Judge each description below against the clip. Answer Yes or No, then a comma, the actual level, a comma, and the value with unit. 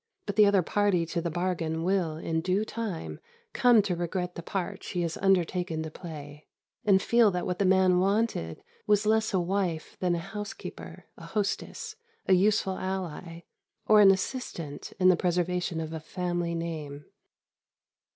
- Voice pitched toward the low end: No, medium, 180 Hz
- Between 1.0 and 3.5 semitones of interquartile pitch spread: Yes, average, 2.9 semitones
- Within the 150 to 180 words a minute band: Yes, average, 165 wpm